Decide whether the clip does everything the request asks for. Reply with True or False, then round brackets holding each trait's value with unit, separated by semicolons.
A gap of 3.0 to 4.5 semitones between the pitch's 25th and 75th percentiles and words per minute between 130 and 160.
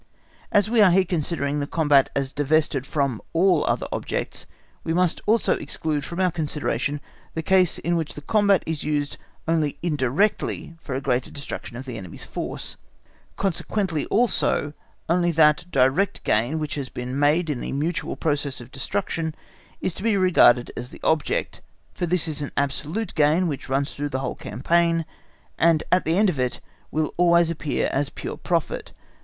False (3.6 semitones; 175 wpm)